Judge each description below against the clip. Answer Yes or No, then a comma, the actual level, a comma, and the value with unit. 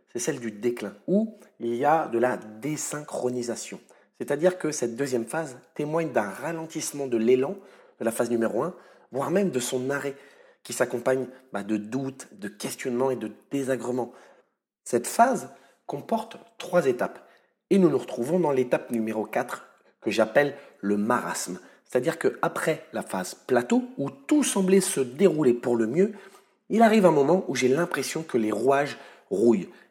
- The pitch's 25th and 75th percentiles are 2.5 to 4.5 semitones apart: No, wide, 5.5 semitones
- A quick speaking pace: No, average, 165 wpm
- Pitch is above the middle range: No, low, 135 Hz